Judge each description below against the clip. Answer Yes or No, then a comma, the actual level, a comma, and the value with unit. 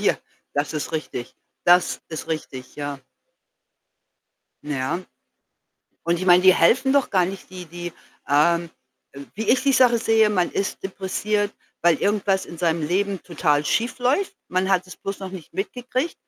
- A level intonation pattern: No, average, 4.0 semitones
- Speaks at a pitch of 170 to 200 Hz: Yes, medium, 185 Hz